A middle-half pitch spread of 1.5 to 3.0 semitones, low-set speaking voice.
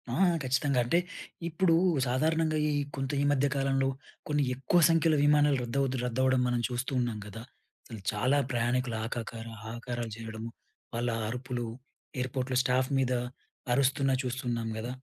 Yes: narrow, 2.5 semitones; low, 125 Hz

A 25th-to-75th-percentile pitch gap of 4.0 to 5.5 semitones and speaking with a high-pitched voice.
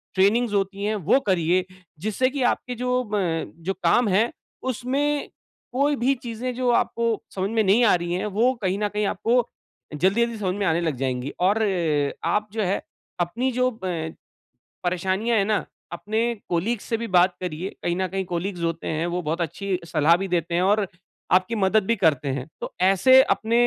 Yes: average, 4.6 semitones; high, 200 Hz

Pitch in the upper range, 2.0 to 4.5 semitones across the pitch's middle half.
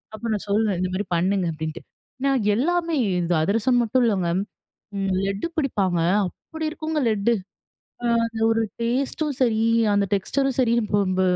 No: high, 215 Hz; average, 5.3 semitones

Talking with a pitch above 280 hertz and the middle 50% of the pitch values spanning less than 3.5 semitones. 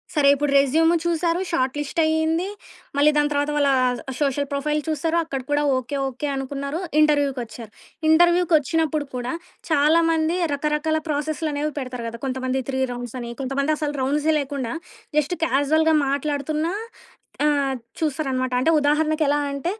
Yes: very high, 290 Hz; narrow, 2.6 semitones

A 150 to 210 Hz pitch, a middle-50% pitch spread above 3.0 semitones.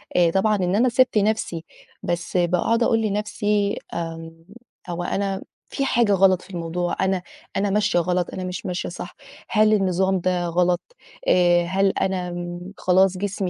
No: medium, 185 Hz; narrow, 2.5 semitones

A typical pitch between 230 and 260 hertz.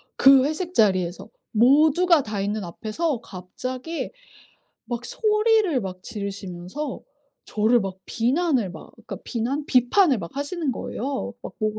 Yes: high, 245 Hz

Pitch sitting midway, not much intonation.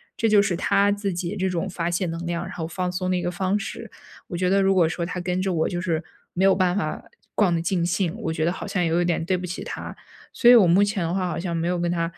Yes: medium, 180 Hz; narrow, 2.0 semitones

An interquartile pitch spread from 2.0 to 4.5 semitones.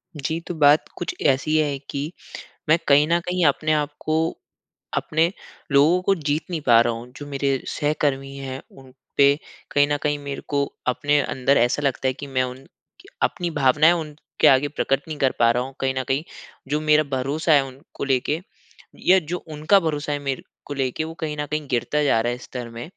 Yes: narrow, 2.4 semitones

